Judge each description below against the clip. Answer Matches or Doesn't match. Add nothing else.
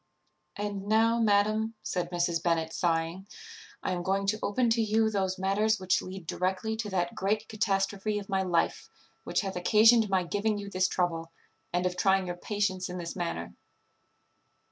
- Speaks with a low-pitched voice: Doesn't match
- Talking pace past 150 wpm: Matches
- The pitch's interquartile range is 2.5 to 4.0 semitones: Matches